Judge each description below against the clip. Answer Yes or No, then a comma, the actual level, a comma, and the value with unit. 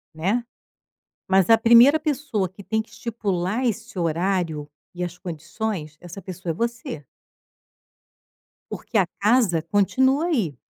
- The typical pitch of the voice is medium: No, high, 195 Hz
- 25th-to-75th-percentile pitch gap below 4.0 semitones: No, average, 5.1 semitones